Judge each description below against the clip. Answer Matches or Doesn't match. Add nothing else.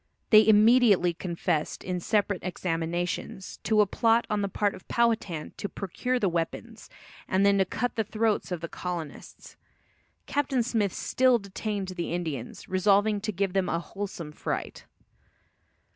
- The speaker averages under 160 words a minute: Matches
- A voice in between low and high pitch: Doesn't match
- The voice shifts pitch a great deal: Doesn't match